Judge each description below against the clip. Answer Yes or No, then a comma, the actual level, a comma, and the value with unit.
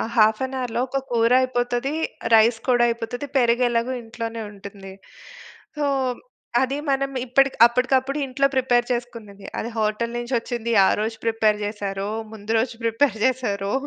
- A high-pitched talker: Yes, high, 235 Hz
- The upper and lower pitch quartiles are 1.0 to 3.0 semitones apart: Yes, narrow, 2.5 semitones